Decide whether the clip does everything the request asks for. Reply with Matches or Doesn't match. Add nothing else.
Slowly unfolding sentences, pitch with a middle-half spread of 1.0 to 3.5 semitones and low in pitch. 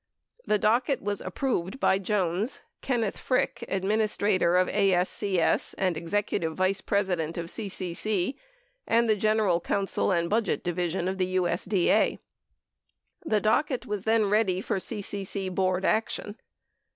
Doesn't match